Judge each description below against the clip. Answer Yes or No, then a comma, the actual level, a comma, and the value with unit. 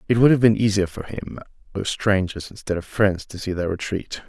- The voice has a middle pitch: No, low, 100 Hz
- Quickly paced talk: Yes, fast, 225 wpm